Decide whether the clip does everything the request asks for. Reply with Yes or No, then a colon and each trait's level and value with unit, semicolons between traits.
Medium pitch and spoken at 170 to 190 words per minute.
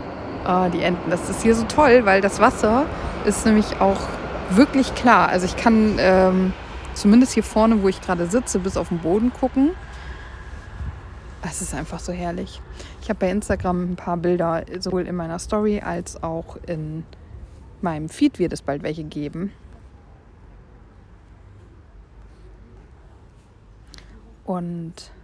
No: medium, 175 Hz; average, 140 wpm